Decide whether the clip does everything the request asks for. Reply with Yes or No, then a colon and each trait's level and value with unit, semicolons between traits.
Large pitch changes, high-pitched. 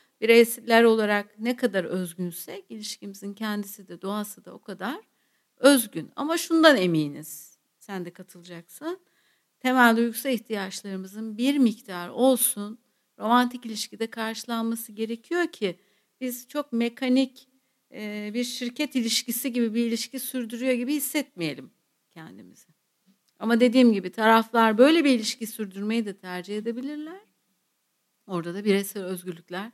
No: average, 4.0 semitones; high, 225 Hz